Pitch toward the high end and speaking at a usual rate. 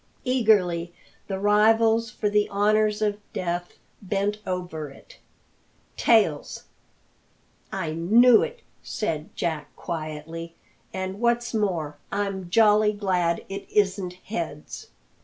No: high, 195 Hz; slow, 105 wpm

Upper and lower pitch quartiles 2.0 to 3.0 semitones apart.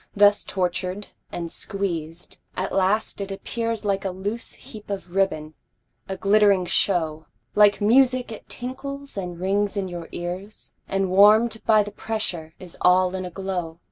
Yes: average, 2.7 semitones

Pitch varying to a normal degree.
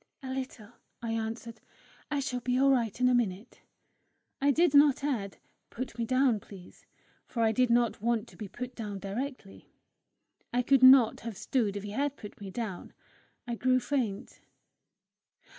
Yes: average, 3.2 semitones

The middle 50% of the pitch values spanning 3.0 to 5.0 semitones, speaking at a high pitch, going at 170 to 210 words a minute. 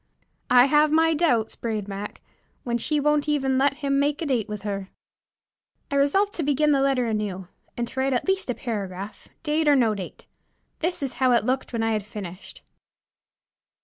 No: wide, 5.4 semitones; very high, 260 Hz; average, 190 wpm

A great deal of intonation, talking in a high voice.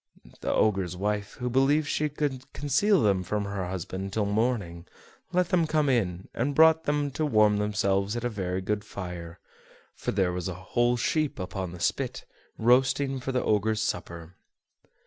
No: wide, 6.2 semitones; low, 105 Hz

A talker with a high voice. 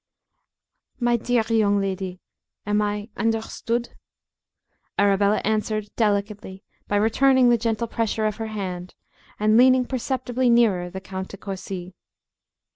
Yes: high, 215 Hz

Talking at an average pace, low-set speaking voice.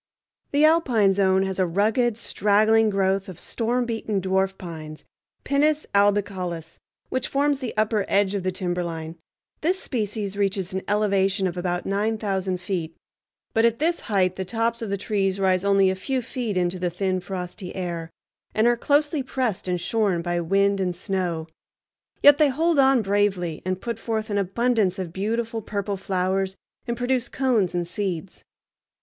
No: average, 165 wpm; high, 200 Hz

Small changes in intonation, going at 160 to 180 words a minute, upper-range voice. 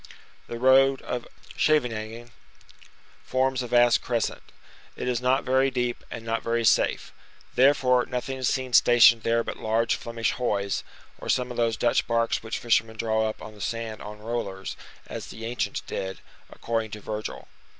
No: narrow, 2.0 semitones; average, 165 wpm; low, 115 Hz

